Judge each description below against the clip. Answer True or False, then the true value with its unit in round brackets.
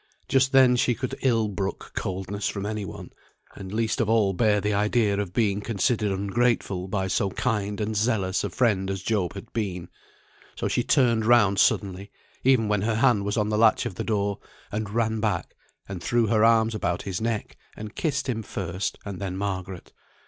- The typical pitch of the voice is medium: False (105 Hz)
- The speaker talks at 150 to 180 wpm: False (190 wpm)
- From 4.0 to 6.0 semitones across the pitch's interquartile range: False (2.6 semitones)